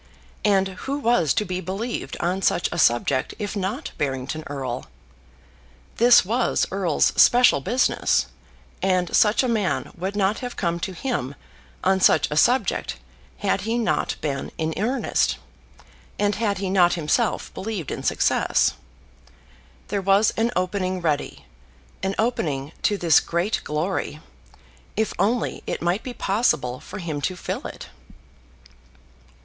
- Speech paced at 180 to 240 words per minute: No, average, 140 wpm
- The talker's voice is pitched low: No, high, 190 Hz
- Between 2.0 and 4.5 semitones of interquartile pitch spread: No, average, 4.9 semitones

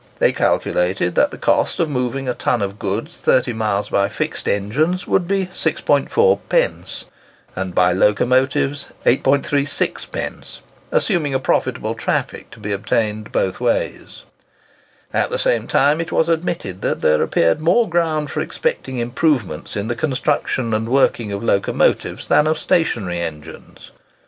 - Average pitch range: No, wide, 7.5 semitones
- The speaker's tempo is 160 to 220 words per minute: No, average, 140 wpm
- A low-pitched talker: Yes, low, 125 Hz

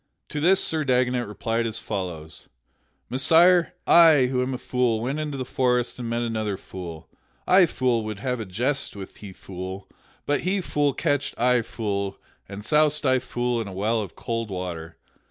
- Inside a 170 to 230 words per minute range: Yes, average, 180 wpm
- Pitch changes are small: No, average, 5.1 semitones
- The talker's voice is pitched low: Yes, low, 120 Hz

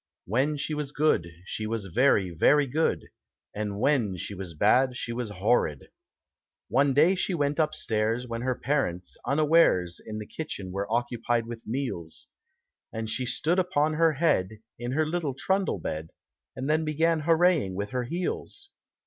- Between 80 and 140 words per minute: No, average, 160 wpm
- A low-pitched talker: Yes, low, 125 Hz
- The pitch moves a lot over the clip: Yes, wide, 6.3 semitones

